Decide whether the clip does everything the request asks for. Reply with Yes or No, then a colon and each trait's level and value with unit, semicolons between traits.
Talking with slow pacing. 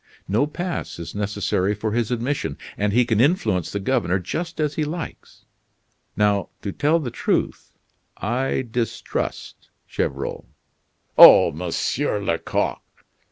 Yes: slow, 125 wpm